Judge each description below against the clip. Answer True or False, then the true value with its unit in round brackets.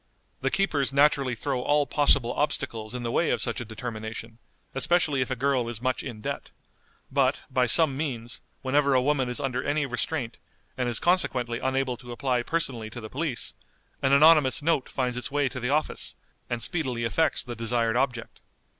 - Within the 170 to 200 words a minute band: True (185 wpm)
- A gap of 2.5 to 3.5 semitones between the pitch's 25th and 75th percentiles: True (3.1 semitones)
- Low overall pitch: True (130 Hz)